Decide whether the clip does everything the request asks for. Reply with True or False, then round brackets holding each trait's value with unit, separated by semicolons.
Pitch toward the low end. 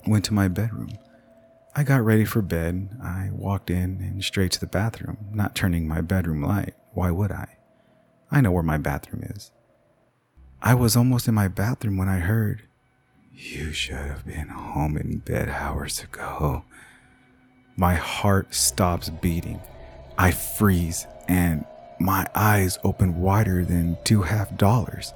True (95 Hz)